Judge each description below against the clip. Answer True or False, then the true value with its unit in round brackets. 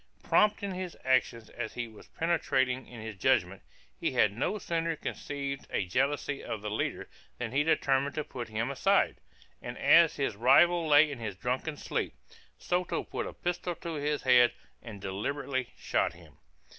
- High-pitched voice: False (135 Hz)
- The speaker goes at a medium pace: True (170 wpm)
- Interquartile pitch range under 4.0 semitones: False (5.6 semitones)